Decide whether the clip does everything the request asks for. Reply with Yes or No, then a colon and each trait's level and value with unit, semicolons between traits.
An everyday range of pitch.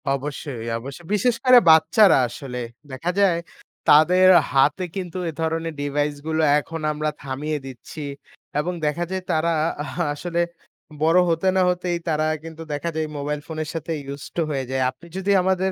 Yes: average, 3.3 semitones